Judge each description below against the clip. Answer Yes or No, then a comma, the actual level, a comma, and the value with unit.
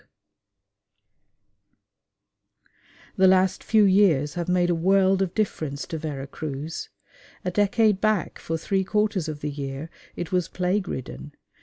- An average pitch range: Yes, average, 4.0 semitones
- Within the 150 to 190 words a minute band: No, slow, 135 wpm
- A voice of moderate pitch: Yes, medium, 180 Hz